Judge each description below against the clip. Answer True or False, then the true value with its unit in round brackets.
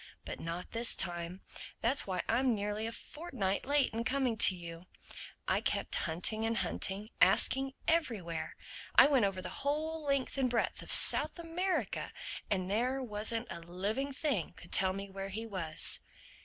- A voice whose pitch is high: True (220 Hz)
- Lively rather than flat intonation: True (6.2 semitones)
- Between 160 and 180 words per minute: True (165 wpm)